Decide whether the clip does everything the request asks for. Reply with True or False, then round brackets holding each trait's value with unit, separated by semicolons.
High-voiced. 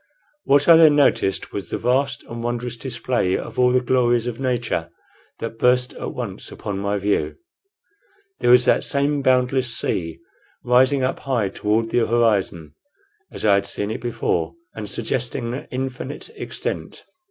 False (120 Hz)